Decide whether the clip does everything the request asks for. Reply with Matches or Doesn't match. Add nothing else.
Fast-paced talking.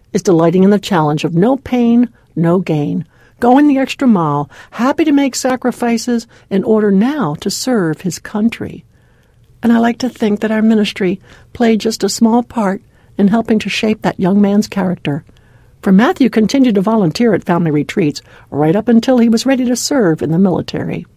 Doesn't match